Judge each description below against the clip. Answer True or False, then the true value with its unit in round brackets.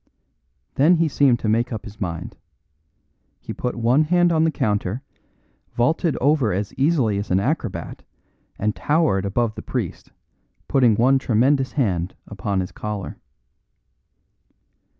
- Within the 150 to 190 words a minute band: False (135 wpm)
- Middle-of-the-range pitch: False (120 Hz)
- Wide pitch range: True (5.7 semitones)